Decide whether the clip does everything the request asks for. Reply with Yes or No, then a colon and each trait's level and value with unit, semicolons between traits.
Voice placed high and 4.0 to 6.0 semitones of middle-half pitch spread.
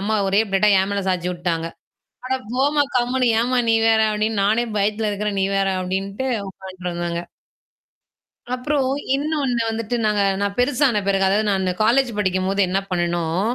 Yes: high, 205 Hz; average, 4.3 semitones